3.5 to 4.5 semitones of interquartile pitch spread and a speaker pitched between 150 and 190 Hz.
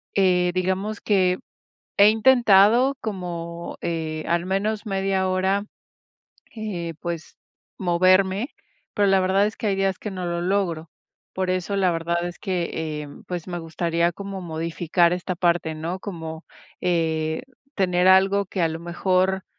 No: narrow, 2.4 semitones; medium, 185 Hz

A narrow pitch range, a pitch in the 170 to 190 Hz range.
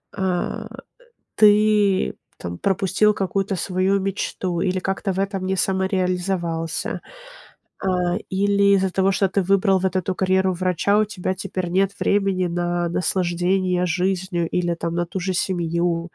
Yes: narrow, 1.7 semitones; medium, 185 Hz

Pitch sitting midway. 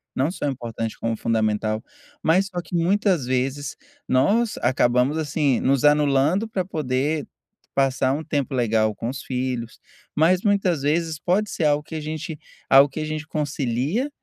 Yes: medium, 145 Hz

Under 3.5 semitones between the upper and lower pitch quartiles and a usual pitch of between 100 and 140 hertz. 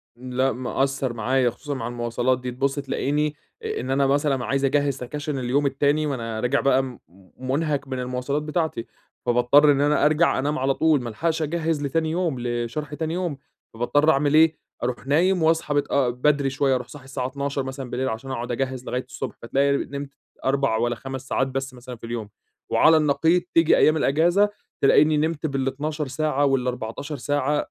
Yes: average, 2.8 semitones; low, 135 Hz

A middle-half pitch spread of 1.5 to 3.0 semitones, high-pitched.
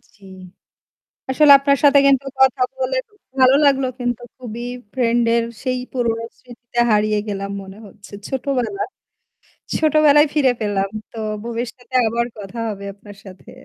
No: average, 4.1 semitones; high, 245 Hz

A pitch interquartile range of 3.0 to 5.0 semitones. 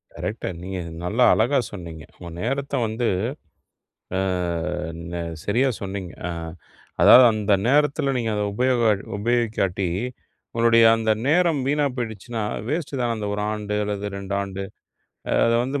Yes: average, 4.1 semitones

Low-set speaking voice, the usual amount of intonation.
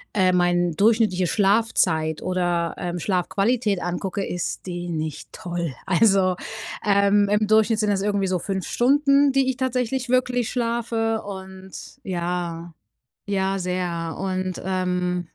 No: high, 190 Hz; average, 3.7 semitones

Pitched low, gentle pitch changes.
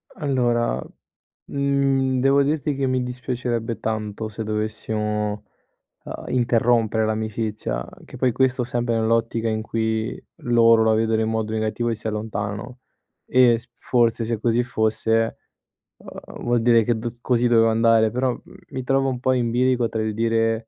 Yes: low, 115 Hz; narrow, 2.0 semitones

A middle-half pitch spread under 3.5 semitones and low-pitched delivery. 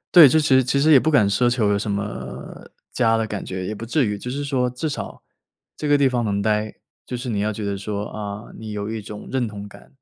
No: average, 3.8 semitones; low, 110 Hz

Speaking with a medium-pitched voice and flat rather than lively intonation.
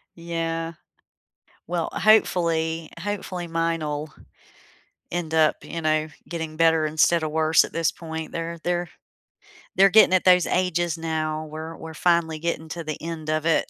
Yes: medium, 165 Hz; narrow, 1.4 semitones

